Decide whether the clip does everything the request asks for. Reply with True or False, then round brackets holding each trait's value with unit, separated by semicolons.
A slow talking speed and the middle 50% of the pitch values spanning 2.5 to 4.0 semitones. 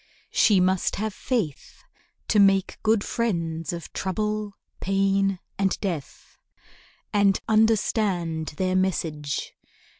True (100 wpm; 3.5 semitones)